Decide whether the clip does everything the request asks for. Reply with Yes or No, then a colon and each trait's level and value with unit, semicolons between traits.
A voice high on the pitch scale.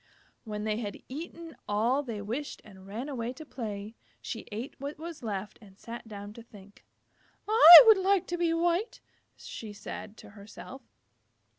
Yes: high, 230 Hz